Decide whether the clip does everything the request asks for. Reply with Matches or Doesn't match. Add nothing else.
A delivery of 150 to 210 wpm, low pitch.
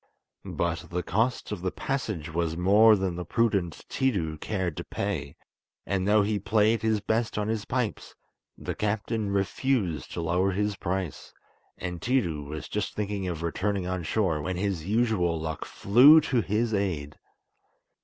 Matches